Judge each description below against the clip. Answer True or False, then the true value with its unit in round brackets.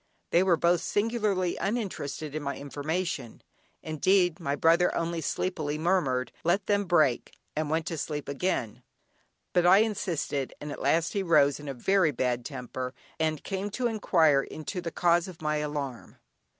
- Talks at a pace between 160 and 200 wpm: True (165 wpm)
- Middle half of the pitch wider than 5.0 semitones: False (4.2 semitones)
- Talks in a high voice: False (165 Hz)